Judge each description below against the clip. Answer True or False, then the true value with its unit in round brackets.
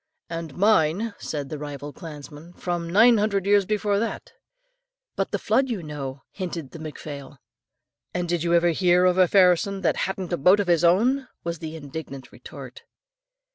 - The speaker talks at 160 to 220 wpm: True (175 wpm)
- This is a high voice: False (175 Hz)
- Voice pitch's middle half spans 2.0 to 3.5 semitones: False (4.2 semitones)